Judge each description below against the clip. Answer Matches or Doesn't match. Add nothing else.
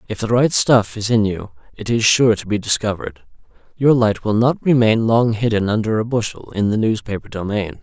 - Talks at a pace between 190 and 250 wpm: Matches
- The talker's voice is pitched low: Matches